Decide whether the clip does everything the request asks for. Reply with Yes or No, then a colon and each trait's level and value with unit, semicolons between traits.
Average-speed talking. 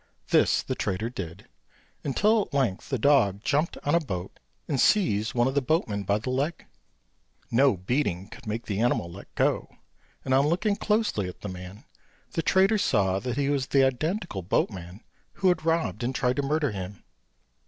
Yes: average, 180 wpm